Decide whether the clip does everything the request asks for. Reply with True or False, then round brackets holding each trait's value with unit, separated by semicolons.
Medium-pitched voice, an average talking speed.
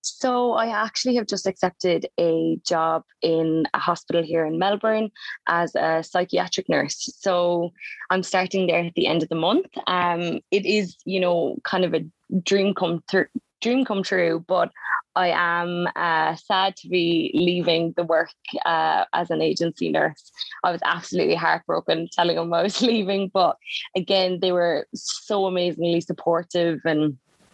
True (175 Hz; 160 wpm)